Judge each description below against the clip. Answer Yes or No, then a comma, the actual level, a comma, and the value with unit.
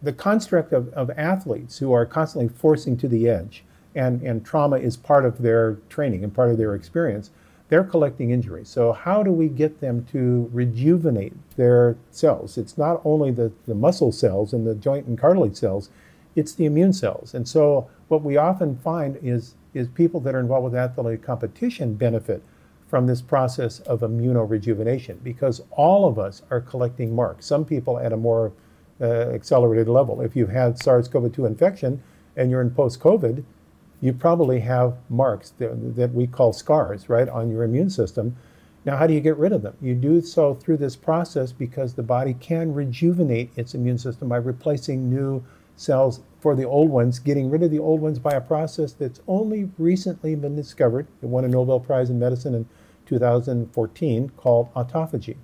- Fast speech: No, average, 185 wpm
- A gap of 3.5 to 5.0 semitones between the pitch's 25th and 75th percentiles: Yes, average, 4.0 semitones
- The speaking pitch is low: Yes, low, 125 Hz